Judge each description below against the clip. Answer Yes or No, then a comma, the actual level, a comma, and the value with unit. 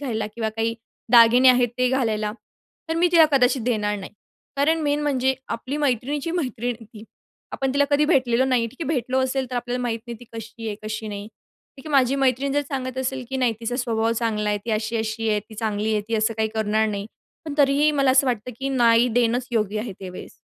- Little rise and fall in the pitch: No, average, 3.4 semitones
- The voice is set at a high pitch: Yes, high, 245 Hz